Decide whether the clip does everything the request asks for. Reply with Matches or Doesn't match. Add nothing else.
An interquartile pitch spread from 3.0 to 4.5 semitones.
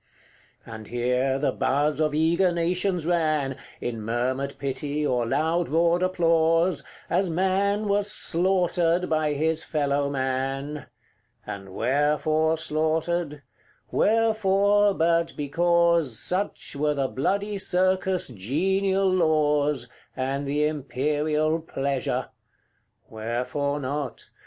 Matches